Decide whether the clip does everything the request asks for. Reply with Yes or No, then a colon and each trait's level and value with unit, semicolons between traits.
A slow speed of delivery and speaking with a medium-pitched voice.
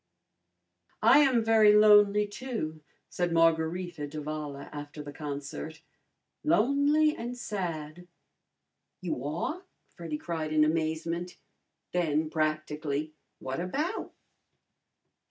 Yes: slow, 95 wpm; medium, 165 Hz